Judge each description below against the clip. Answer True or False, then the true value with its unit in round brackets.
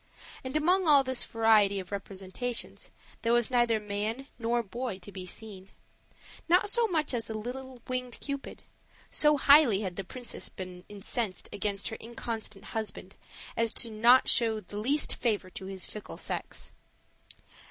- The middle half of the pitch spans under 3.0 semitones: False (4.1 semitones)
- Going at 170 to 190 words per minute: False (155 wpm)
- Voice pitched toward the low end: False (225 Hz)